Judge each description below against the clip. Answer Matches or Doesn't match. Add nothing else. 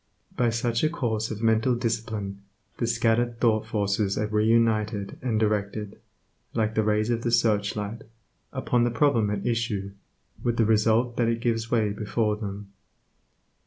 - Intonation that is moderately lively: Doesn't match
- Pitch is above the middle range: Doesn't match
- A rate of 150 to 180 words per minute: Matches